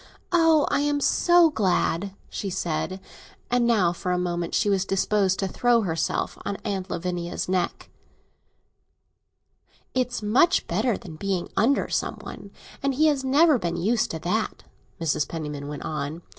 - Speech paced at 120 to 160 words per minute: Yes, average, 150 wpm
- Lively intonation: Yes, wide, 6.3 semitones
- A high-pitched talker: Yes, high, 195 Hz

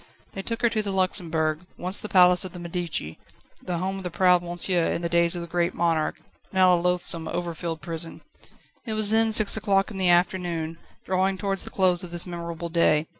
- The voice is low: No, medium, 175 Hz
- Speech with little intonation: Yes, narrow, 1.9 semitones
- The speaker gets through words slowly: No, fast, 205 wpm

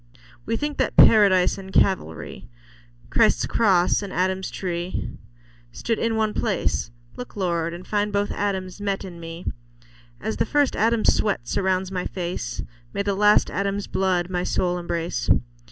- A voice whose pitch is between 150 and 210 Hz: Yes, high, 190 Hz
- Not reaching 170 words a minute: Yes, average, 155 wpm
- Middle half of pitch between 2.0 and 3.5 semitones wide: Yes, narrow, 2.5 semitones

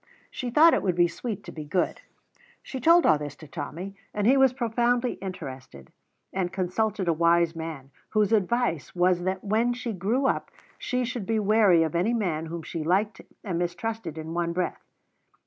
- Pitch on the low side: No, high, 190 Hz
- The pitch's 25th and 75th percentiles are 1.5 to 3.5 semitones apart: No, average, 5.2 semitones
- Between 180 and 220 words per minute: Yes, average, 185 wpm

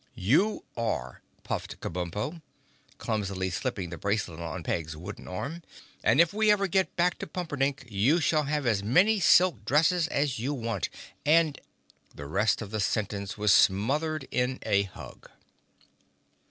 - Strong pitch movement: Yes, wide, 8.3 semitones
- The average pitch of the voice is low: Yes, low, 125 Hz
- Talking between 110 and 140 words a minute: No, average, 150 wpm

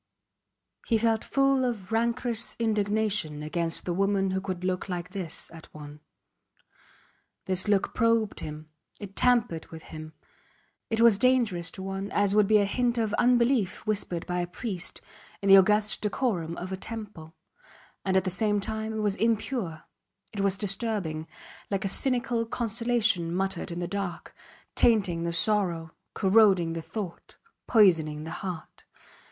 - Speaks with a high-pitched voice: Yes, high, 195 Hz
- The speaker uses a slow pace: No, average, 155 wpm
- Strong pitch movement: No, average, 4.2 semitones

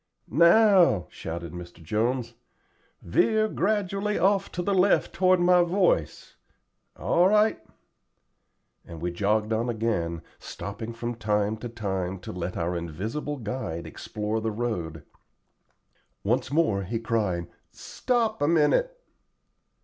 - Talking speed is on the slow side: Yes, slow, 120 wpm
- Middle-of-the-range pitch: No, low, 115 Hz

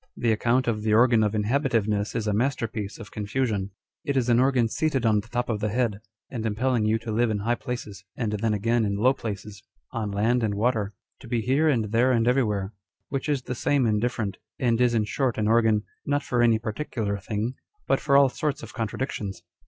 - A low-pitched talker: Yes, low, 115 Hz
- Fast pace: Yes, fast, 220 wpm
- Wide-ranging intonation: No, average, 2.9 semitones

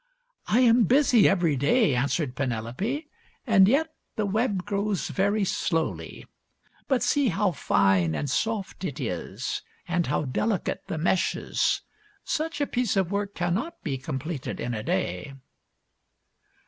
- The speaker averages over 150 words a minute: No, average, 145 wpm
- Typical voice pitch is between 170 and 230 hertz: Yes, high, 190 Hz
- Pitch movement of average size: No, wide, 8.1 semitones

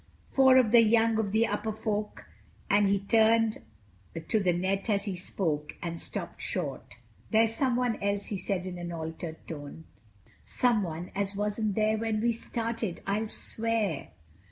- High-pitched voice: Yes, high, 210 Hz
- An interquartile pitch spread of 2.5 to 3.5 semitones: Yes, average, 3.2 semitones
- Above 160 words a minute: No, average, 155 wpm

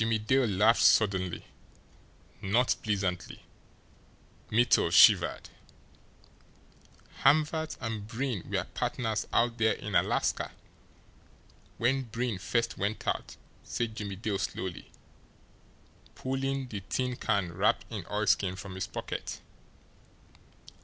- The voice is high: No, low, 110 Hz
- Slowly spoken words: Yes, slow, 105 wpm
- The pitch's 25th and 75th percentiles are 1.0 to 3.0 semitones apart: No, average, 4.0 semitones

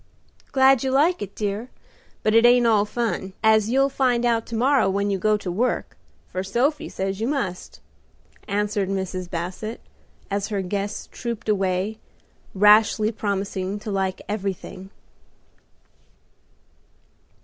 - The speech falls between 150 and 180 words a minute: No, slow, 135 wpm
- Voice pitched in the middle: No, high, 210 Hz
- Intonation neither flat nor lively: Yes, average, 3.3 semitones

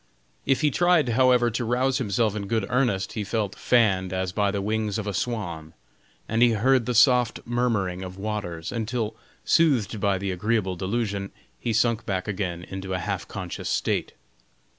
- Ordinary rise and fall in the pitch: Yes, average, 3.9 semitones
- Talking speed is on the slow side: No, average, 175 wpm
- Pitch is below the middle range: Yes, low, 105 Hz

